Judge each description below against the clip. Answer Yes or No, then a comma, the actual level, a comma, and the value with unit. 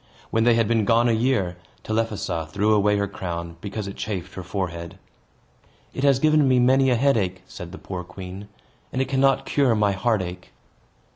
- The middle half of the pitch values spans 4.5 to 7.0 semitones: Yes, average, 4.8 semitones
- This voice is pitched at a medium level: No, low, 105 Hz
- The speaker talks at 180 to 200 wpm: Yes, average, 185 wpm